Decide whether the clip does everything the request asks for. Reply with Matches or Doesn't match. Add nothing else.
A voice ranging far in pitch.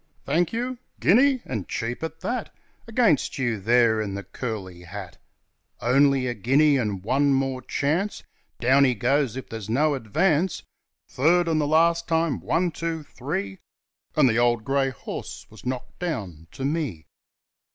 Matches